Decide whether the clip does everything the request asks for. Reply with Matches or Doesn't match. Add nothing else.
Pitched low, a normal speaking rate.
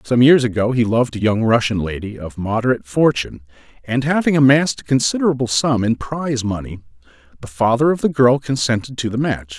Matches